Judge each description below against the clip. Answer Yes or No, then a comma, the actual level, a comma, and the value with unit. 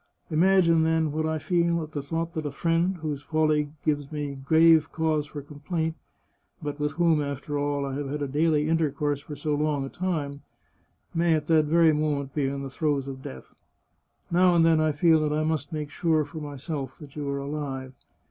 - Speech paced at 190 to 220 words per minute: Yes, fast, 205 wpm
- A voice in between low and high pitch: Yes, medium, 150 Hz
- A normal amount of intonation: No, narrow, 2.0 semitones